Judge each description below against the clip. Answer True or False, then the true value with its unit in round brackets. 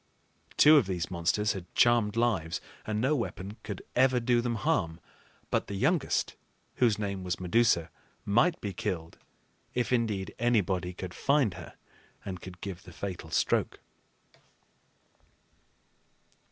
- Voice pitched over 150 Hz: False (100 Hz)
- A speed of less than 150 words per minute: True (135 wpm)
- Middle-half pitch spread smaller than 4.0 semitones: False (4.7 semitones)